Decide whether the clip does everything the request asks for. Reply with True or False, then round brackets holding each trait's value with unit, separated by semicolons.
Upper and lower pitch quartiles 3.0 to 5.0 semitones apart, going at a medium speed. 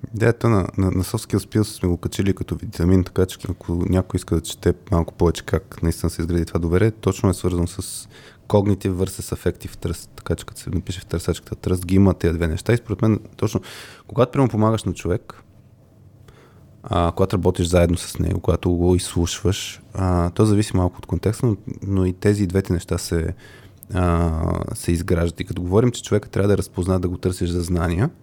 False (3.4 semitones; 200 wpm)